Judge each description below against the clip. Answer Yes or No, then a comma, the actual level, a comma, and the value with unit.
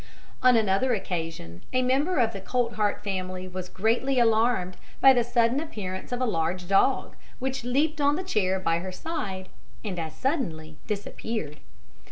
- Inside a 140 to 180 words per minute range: Yes, average, 160 wpm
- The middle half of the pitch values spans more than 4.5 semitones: Yes, wide, 5.6 semitones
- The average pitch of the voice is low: No, high, 215 Hz